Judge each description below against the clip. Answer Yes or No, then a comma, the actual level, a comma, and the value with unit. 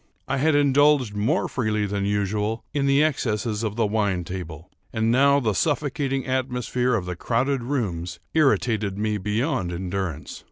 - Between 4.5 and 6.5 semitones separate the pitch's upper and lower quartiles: Yes, average, 5.0 semitones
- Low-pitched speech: Yes, low, 110 Hz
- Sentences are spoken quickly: No, average, 155 wpm